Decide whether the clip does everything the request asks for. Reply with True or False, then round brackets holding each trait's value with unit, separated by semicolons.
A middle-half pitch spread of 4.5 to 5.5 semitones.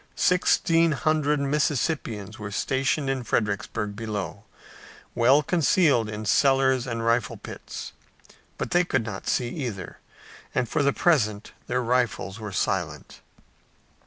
True (5.2 semitones)